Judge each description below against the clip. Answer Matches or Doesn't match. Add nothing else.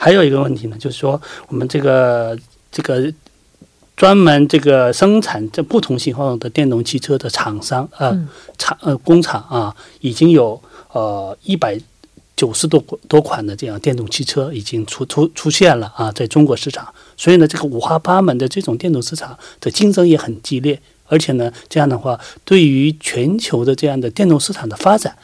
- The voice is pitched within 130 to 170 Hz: Matches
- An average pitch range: Matches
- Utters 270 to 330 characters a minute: Matches